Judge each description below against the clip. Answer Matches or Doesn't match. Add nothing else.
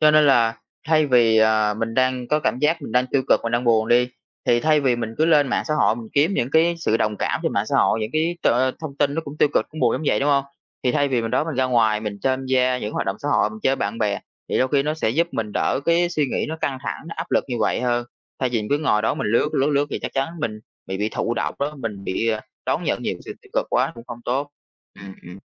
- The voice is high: Doesn't match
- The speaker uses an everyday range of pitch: Matches